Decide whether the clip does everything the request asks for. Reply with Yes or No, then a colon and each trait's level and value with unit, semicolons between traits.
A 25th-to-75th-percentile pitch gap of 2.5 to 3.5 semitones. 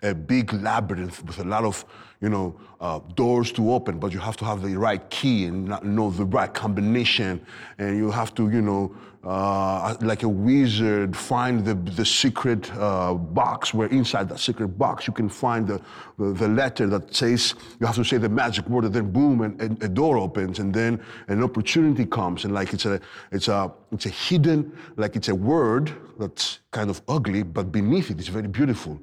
Yes: average, 3.0 semitones